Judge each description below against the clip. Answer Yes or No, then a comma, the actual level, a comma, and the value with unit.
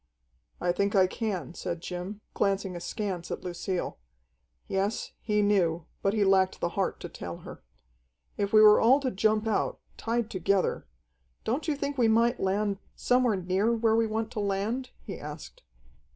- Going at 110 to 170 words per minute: Yes, average, 165 wpm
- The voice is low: No, high, 200 Hz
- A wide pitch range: No, average, 3.3 semitones